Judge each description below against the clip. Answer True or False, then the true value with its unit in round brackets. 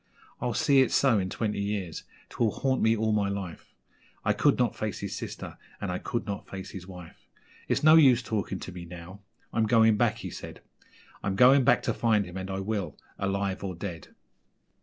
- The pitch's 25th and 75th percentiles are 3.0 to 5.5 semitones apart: True (3.3 semitones)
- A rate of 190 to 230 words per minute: True (200 wpm)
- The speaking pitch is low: True (100 Hz)